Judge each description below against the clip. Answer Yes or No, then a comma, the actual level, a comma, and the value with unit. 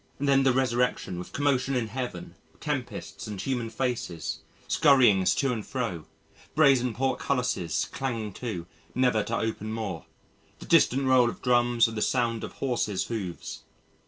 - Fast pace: No, average, 145 wpm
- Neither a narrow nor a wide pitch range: Yes, average, 3.5 semitones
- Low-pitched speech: Yes, low, 120 Hz